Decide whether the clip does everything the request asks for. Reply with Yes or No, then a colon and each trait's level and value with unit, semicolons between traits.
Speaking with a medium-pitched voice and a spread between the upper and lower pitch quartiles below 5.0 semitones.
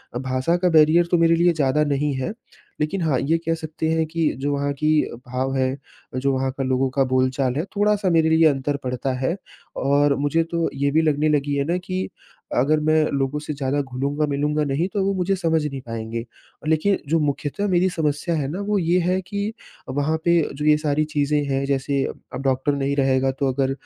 Yes: medium, 150 Hz; average, 3.4 semitones